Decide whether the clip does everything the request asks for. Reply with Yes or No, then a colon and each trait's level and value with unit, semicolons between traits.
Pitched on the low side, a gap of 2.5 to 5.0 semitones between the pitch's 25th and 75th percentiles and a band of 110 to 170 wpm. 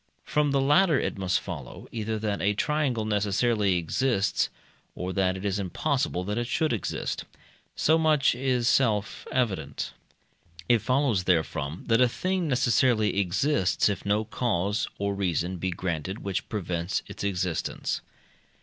No: low, 105 Hz; wide, 5.4 semitones; average, 145 wpm